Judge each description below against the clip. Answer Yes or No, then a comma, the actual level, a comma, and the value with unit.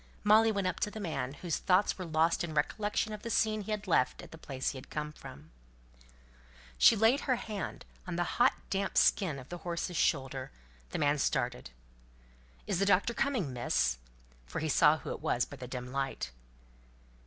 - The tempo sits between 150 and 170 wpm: No, average, 195 wpm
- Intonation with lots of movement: Yes, wide, 7.2 semitones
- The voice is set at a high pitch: No, medium, 170 Hz